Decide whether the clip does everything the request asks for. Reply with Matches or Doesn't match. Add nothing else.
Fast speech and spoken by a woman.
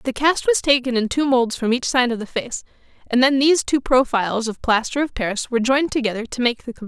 Matches